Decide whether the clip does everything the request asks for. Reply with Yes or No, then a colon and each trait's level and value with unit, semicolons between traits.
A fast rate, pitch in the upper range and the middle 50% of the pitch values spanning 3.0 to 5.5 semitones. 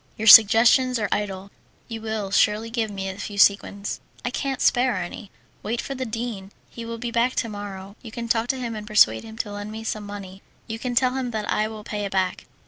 No: fast, 230 wpm; high, 220 Hz; narrow, 2.5 semitones